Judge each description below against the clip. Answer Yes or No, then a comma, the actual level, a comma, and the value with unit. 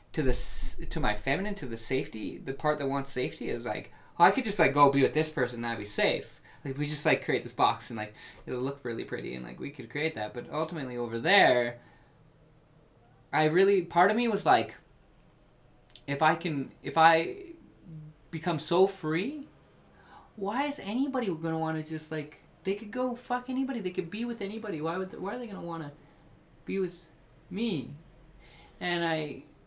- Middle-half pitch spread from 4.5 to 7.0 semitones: Yes, average, 5.2 semitones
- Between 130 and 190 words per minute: No, average, 200 wpm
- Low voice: No, medium, 155 Hz